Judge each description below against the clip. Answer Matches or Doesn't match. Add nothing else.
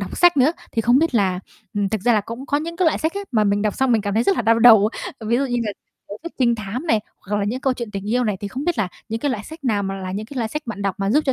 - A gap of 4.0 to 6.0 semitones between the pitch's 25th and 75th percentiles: Matches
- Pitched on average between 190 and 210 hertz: Doesn't match